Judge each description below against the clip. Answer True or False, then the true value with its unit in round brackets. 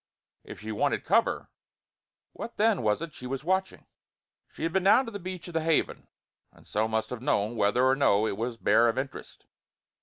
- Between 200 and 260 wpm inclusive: True (205 wpm)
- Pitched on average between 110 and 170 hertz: True (135 Hz)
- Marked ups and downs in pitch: True (8.1 semitones)